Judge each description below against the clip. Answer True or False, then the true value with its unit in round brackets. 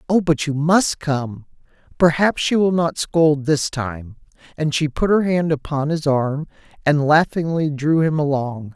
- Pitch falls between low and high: True (150 Hz)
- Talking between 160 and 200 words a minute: True (170 wpm)